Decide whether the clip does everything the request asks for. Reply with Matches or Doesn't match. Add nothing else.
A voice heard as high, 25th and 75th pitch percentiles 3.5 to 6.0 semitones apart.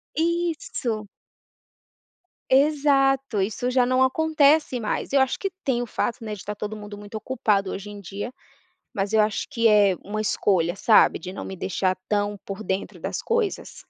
Matches